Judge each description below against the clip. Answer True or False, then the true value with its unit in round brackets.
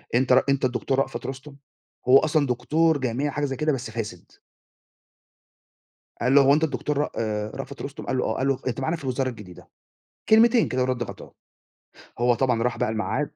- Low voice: True (130 Hz)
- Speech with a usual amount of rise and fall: True (3.0 semitones)